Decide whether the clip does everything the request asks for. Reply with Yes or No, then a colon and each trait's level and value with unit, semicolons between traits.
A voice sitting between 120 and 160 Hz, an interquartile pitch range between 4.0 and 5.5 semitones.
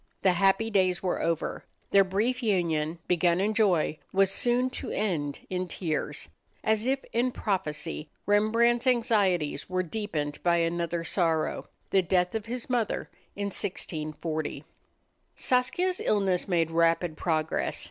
No: medium, 185 Hz; average, 4.6 semitones